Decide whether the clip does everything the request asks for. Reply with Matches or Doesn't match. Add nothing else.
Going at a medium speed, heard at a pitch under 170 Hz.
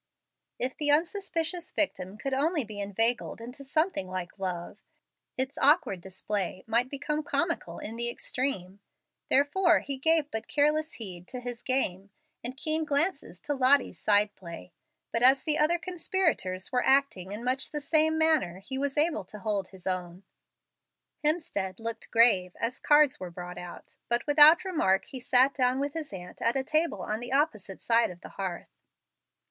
Doesn't match